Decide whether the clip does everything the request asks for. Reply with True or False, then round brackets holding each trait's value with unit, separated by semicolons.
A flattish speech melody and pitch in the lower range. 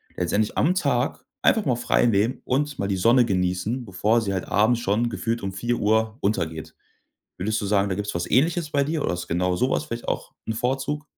False (4.5 semitones; 110 Hz)